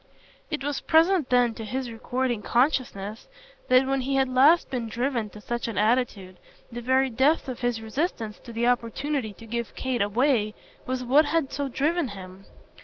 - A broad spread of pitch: No, average, 3.2 semitones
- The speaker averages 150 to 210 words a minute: Yes, average, 180 wpm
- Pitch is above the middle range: Yes, very high, 250 Hz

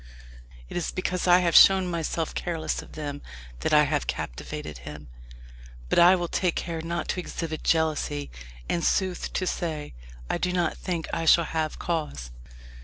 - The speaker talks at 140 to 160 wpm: No, average, 170 wpm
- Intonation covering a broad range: No, average, 2.7 semitones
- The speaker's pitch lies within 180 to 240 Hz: No, medium, 165 Hz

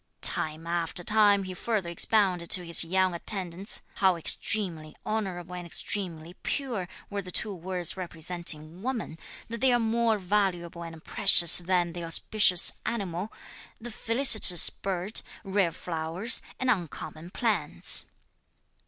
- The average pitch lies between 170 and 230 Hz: Yes, medium, 185 Hz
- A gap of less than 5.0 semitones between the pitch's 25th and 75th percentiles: Yes, average, 3.7 semitones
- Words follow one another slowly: Yes, slow, 130 wpm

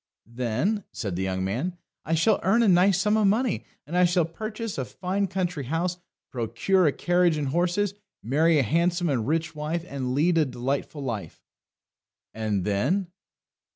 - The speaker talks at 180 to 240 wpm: No, average, 170 wpm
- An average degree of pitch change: No, wide, 6.1 semitones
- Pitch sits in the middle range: Yes, medium, 165 Hz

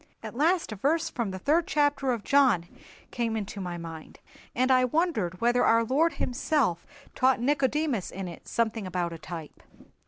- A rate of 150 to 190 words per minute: Yes, average, 175 wpm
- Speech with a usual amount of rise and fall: No, wide, 7.1 semitones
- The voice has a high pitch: Yes, high, 240 Hz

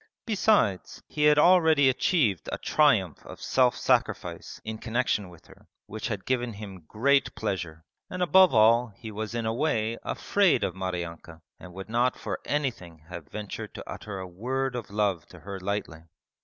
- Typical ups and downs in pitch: No, wide, 5.9 semitones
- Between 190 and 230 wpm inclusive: No, average, 170 wpm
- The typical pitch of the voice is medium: No, low, 110 Hz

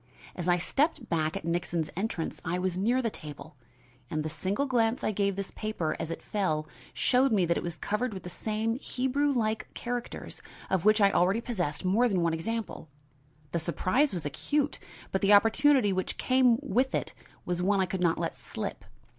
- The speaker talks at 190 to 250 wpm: Yes, average, 195 wpm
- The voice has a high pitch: Yes, high, 200 Hz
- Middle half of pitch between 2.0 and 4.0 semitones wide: No, wide, 5.4 semitones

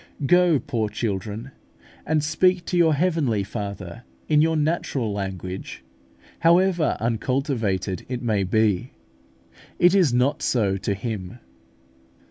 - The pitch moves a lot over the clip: Yes, wide, 7.7 semitones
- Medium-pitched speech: No, low, 120 Hz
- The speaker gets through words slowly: Yes, slow, 115 wpm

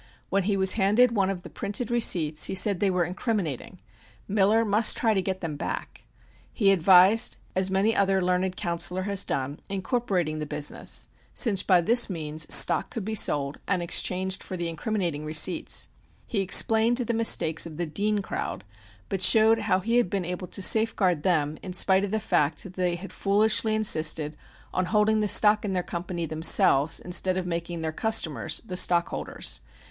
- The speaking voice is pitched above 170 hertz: Yes, high, 190 Hz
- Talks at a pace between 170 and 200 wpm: Yes, average, 180 wpm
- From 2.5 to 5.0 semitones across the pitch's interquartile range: Yes, average, 3.6 semitones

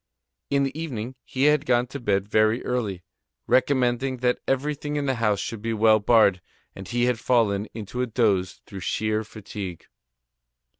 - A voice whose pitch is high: No, low, 115 Hz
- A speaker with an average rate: Yes, average, 165 wpm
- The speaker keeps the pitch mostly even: No, average, 3.6 semitones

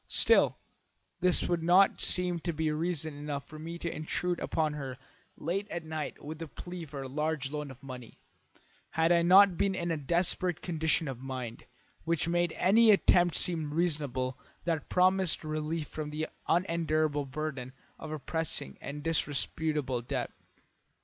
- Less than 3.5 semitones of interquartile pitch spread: Yes, average, 2.9 semitones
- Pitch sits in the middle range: Yes, medium, 160 Hz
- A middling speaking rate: Yes, average, 160 wpm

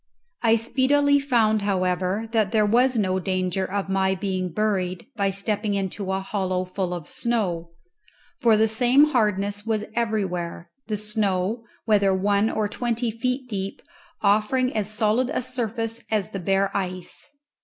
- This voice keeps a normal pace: Yes, average, 150 wpm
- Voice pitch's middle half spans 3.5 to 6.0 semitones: No, average, 3.1 semitones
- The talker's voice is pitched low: No, high, 210 Hz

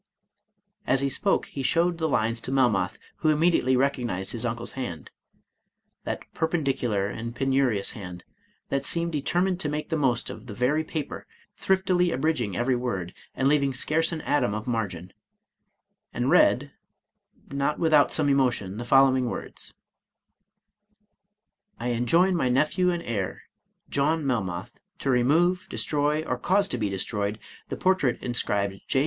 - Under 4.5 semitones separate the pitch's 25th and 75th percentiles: No, average, 5.2 semitones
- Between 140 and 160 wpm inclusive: Yes, average, 150 wpm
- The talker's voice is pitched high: No, low, 130 Hz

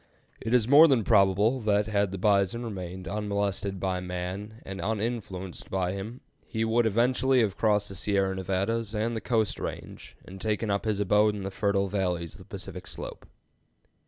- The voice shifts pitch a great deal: No, average, 2.7 semitones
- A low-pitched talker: Yes, low, 100 Hz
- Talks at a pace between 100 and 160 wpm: No, average, 180 wpm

